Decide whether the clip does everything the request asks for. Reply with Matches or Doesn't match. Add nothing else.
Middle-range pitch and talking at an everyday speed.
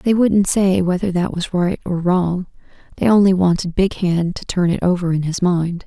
Doesn't match